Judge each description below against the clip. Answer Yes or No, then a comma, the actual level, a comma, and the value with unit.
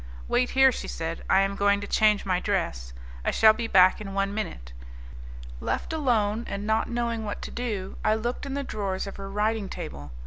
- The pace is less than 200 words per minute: No, fast, 205 wpm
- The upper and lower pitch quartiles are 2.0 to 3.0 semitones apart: Yes, narrow, 2.6 semitones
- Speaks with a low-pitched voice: No, high, 205 Hz